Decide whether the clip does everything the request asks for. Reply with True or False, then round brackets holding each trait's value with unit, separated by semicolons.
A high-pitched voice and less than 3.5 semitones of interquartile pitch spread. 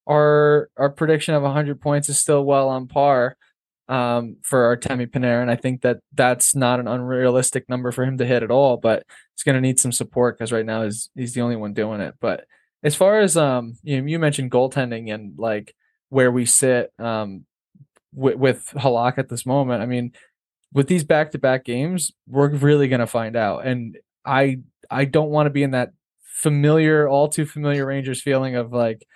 False (130 Hz; 3.0 semitones)